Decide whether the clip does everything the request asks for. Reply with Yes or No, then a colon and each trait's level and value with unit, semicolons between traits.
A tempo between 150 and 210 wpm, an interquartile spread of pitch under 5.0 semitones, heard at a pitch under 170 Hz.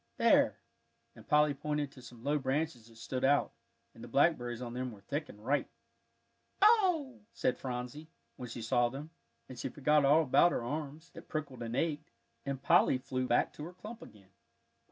Yes: average, 185 wpm; average, 3.8 semitones; low, 135 Hz